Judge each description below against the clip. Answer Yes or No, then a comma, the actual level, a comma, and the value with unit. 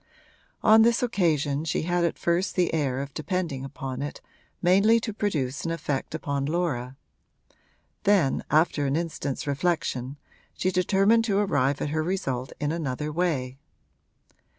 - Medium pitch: Yes, medium, 160 Hz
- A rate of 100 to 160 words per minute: Yes, average, 145 wpm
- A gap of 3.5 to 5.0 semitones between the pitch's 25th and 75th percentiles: Yes, average, 4.7 semitones